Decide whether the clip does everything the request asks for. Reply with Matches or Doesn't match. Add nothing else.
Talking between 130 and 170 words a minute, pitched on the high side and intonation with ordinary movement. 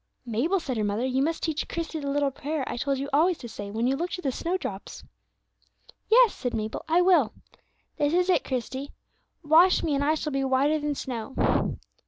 Doesn't match